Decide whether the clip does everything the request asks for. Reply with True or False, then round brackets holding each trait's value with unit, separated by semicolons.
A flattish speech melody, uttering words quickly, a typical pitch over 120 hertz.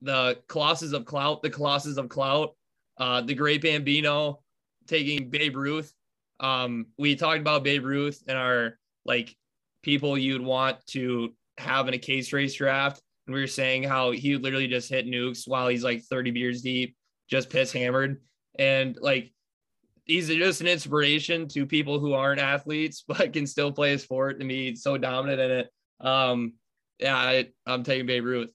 False (2.3 semitones; 175 wpm; 135 Hz)